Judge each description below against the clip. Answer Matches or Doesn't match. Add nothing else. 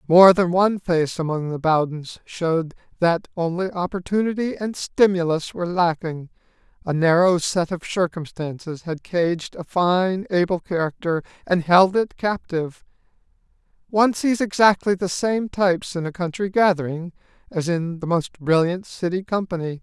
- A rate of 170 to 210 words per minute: Doesn't match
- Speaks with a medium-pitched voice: Matches